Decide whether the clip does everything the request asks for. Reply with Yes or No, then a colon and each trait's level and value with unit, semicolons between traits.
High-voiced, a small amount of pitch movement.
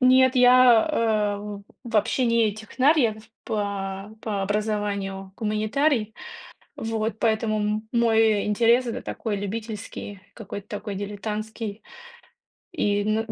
Yes: high, 215 Hz; narrow, 2.0 semitones